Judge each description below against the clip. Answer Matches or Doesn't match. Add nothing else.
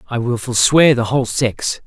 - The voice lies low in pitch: Matches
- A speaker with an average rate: Matches